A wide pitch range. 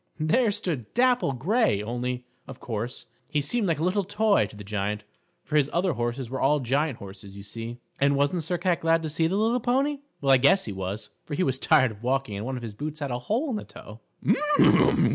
Yes: wide, 7.3 semitones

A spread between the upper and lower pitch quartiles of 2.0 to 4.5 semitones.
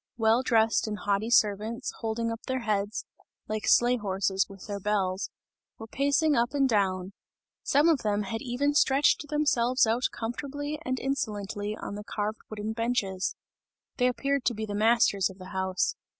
Yes: average, 3.7 semitones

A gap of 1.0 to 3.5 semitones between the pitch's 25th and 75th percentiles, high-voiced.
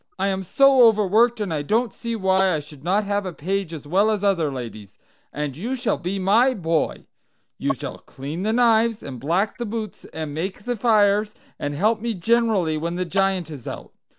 No: average, 5.3 semitones; high, 195 Hz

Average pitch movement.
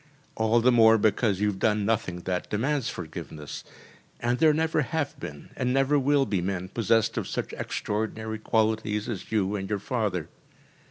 Yes: average, 3.8 semitones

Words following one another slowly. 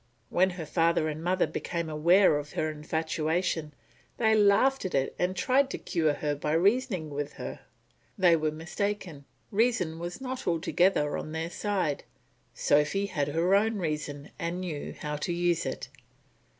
No: average, 160 wpm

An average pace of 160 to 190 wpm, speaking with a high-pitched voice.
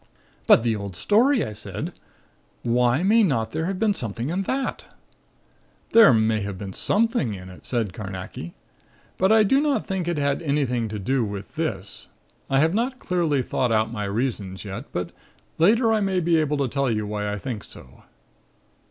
No: average, 185 wpm; low, 130 Hz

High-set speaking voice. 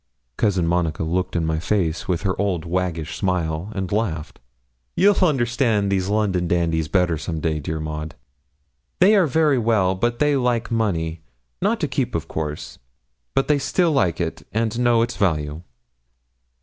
No: very low, 95 Hz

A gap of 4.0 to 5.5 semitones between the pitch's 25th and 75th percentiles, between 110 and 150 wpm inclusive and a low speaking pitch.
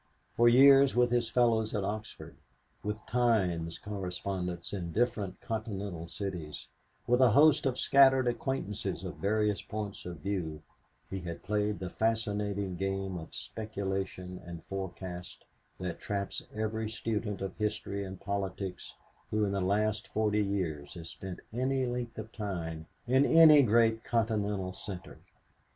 No: average, 3.3 semitones; average, 140 wpm; low, 105 Hz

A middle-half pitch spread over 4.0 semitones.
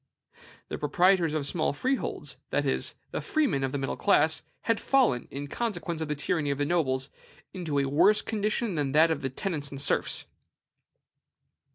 Yes: wide, 5.5 semitones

